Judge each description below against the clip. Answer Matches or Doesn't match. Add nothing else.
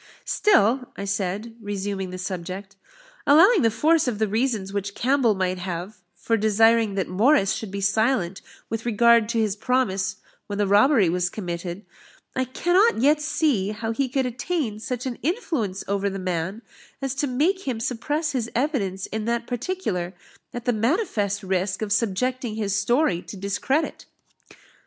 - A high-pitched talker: Matches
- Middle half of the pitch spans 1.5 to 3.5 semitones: Doesn't match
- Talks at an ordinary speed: Matches